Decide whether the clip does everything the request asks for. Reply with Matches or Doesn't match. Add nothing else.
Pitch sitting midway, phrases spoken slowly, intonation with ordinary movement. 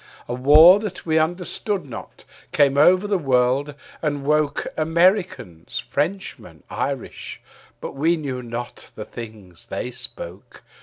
Doesn't match